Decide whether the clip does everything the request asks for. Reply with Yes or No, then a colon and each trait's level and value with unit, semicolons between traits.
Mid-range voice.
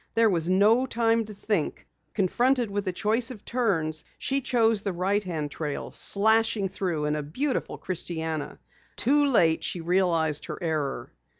No: high, 195 Hz